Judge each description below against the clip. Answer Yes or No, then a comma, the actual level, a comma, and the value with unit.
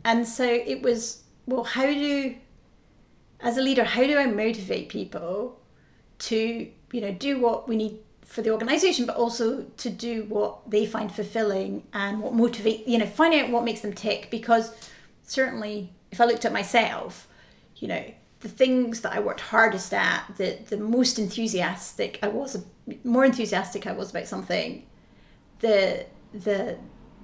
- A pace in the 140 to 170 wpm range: Yes, average, 165 wpm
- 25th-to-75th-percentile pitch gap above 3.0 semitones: No, narrow, 2.5 semitones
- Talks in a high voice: Yes, high, 230 Hz